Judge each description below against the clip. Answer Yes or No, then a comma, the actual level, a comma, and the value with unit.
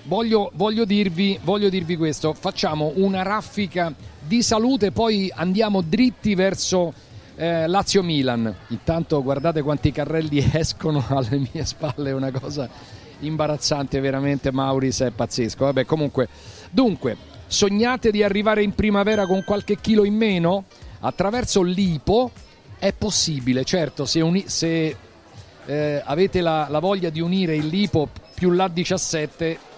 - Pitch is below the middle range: No, medium, 165 Hz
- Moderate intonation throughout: No, wide, 5.7 semitones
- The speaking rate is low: No, average, 135 wpm